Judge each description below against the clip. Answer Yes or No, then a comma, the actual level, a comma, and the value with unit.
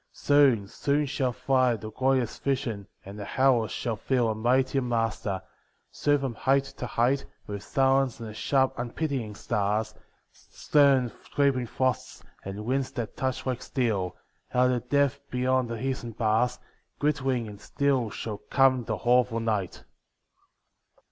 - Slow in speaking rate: No, average, 150 wpm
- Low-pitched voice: Yes, low, 125 Hz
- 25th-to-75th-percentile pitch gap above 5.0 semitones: No, average, 3.2 semitones